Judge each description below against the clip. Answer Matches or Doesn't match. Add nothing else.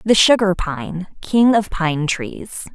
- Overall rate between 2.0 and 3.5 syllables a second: Matches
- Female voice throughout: Matches